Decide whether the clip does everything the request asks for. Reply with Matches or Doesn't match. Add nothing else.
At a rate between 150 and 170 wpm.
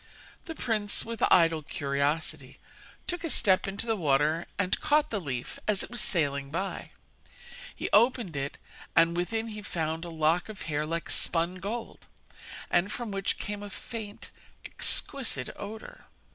Matches